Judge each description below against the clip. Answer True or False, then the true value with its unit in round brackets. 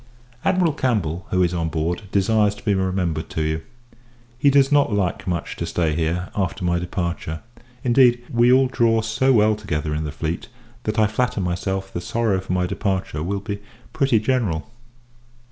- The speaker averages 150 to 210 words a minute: True (180 wpm)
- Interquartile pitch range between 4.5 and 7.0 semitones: True (4.9 semitones)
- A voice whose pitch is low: True (95 Hz)